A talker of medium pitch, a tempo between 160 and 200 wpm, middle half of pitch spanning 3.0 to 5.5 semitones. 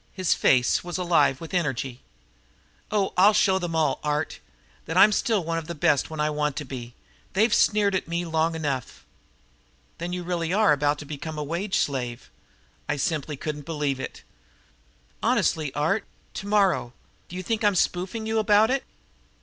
Yes: medium, 165 Hz; average, 175 wpm; average, 4.5 semitones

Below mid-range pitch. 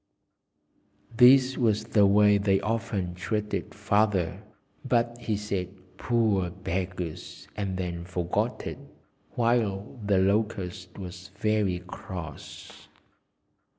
Yes: low, 100 Hz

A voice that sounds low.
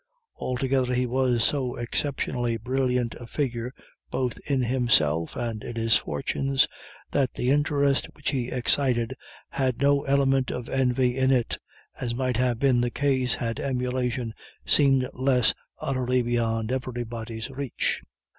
Yes: low, 125 Hz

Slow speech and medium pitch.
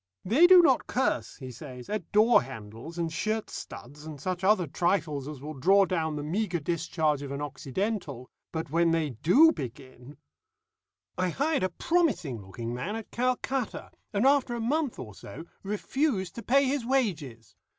No: average, 170 wpm; medium, 170 Hz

